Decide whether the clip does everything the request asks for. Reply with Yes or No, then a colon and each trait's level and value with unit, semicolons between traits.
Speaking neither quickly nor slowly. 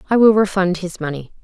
No: fast, 210 wpm